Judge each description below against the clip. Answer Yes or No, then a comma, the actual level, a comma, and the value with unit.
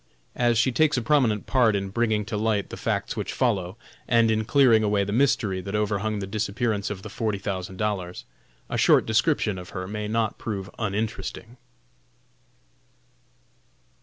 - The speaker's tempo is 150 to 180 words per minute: Yes, average, 165 wpm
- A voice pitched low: Yes, low, 105 Hz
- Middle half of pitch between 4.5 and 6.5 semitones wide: No, narrow, 2.4 semitones